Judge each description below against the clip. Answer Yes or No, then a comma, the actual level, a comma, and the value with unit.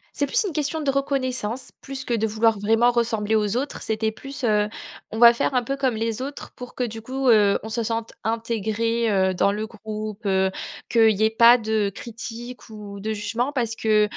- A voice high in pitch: Yes, high, 225 Hz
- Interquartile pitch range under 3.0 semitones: Yes, narrow, 2.5 semitones